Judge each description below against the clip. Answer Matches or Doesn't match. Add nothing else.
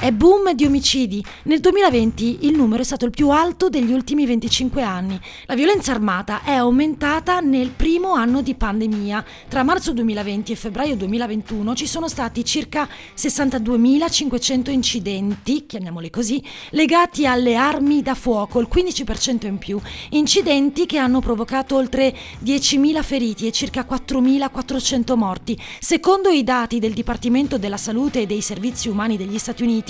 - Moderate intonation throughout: Matches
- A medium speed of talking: Matches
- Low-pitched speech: Doesn't match